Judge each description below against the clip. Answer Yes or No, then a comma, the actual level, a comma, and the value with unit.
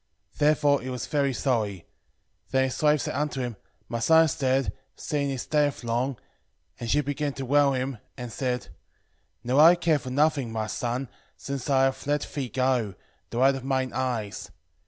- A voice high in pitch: No, low, 135 Hz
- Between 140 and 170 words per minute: No, average, 195 wpm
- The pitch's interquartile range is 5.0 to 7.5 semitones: No, average, 2.7 semitones